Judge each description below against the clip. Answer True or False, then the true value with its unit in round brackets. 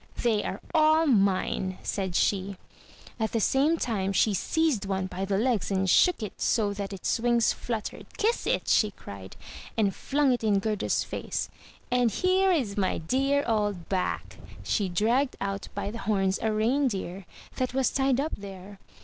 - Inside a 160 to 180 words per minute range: True (170 wpm)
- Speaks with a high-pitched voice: True (215 Hz)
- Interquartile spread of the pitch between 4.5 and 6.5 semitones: True (4.9 semitones)